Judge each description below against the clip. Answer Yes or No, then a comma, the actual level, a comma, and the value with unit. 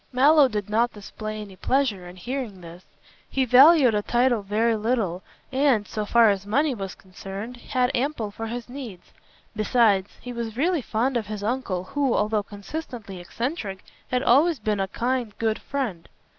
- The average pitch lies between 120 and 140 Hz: No, high, 225 Hz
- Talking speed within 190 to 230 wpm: No, average, 170 wpm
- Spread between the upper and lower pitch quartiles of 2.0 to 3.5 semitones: No, average, 4.0 semitones